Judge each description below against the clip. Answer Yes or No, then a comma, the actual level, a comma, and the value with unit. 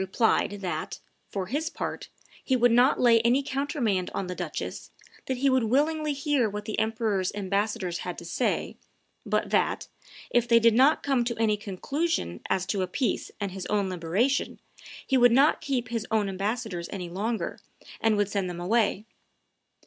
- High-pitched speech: Yes, high, 225 Hz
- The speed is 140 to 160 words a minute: No, average, 175 wpm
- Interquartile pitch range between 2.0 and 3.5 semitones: No, average, 4.7 semitones